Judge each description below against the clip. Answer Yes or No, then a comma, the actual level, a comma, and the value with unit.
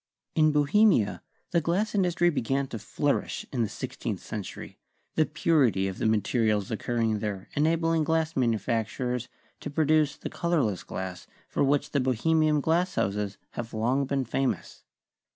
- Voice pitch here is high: No, low, 135 Hz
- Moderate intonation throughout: No, wide, 6.2 semitones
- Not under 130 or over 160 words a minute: Yes, average, 150 wpm